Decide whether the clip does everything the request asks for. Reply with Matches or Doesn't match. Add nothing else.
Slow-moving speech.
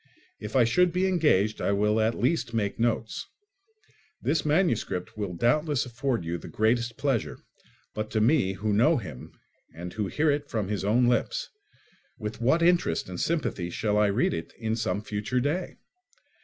Doesn't match